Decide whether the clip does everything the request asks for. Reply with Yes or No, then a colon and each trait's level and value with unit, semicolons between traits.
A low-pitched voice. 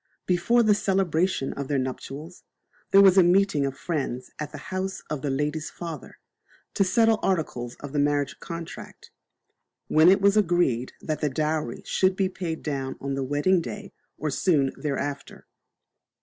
No: medium, 155 Hz